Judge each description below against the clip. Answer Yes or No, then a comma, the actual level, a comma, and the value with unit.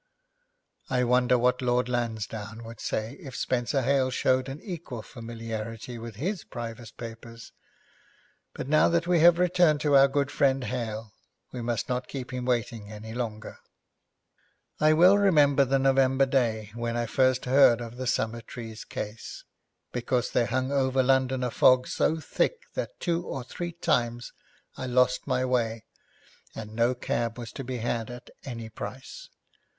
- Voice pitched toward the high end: No, low, 125 Hz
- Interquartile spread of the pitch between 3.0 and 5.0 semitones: No, narrow, 2.6 semitones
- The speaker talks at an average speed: Yes, average, 160 wpm